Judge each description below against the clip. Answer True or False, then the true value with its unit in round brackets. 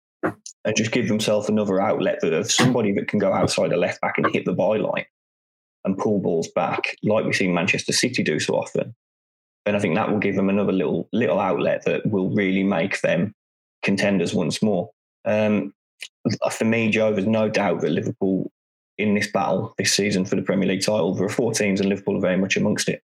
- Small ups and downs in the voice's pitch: True (1.8 semitones)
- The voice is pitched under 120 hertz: True (105 Hz)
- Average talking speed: False (210 wpm)